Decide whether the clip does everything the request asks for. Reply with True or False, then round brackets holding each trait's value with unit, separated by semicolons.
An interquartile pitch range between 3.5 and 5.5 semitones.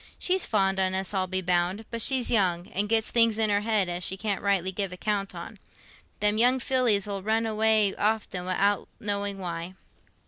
False (2.7 semitones)